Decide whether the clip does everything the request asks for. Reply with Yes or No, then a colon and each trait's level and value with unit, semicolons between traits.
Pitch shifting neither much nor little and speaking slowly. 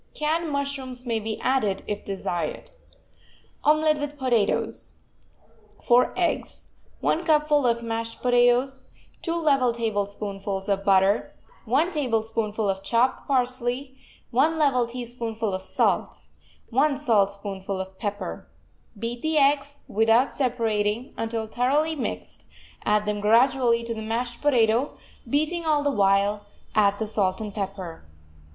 Yes: average, 4.8 semitones; slow, 125 wpm